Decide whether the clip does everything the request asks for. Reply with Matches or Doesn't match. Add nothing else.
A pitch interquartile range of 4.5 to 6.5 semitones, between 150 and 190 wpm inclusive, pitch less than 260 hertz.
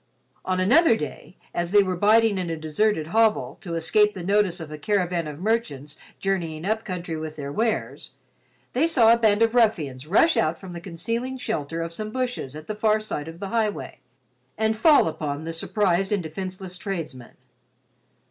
Matches